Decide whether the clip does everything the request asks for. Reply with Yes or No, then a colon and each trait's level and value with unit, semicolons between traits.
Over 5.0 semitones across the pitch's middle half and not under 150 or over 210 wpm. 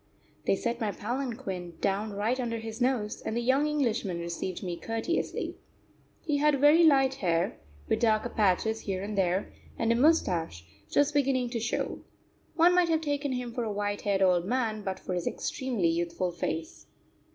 Yes: wide, 5.6 semitones; average, 175 wpm